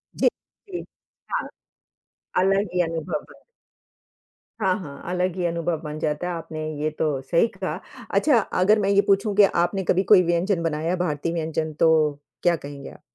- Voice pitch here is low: No, medium, 170 Hz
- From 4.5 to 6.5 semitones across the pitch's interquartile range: No, average, 3.6 semitones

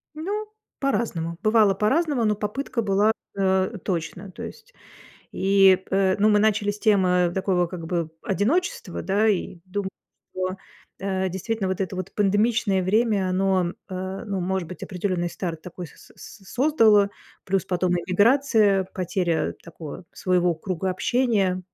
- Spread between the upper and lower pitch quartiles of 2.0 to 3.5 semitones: Yes, narrow, 2.5 semitones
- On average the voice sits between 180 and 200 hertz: Yes, high, 190 Hz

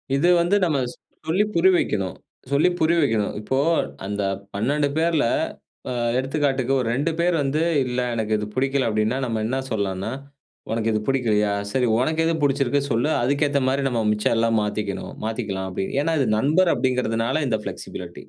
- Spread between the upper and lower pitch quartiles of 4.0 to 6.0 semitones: Yes, average, 5.0 semitones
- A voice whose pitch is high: No, low, 130 Hz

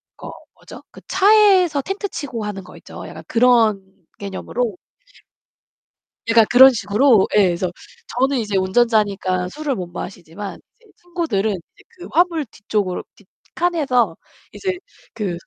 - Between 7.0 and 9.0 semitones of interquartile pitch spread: Yes, wide, 7.7 semitones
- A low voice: No, high, 230 Hz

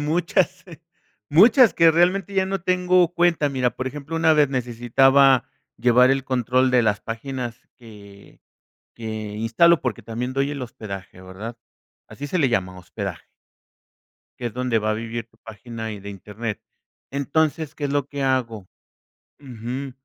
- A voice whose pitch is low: Yes, low, 130 Hz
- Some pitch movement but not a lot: Yes, average, 4.7 semitones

